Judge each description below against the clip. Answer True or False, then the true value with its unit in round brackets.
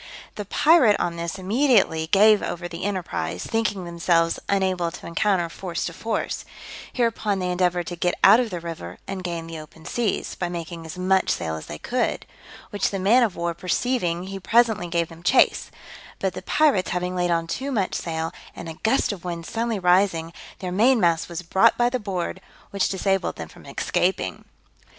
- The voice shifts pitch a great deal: False (3.5 semitones)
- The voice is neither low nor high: True (180 Hz)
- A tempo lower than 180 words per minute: False (190 wpm)